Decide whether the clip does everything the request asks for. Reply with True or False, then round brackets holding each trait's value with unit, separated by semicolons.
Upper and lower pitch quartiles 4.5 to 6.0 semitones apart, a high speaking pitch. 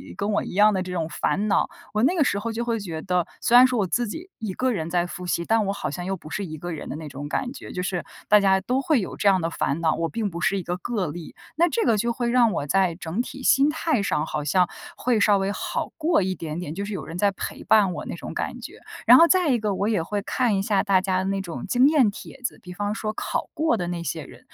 True (4.8 semitones; 200 Hz)